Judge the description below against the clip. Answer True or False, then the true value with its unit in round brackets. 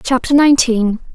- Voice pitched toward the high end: True (250 Hz)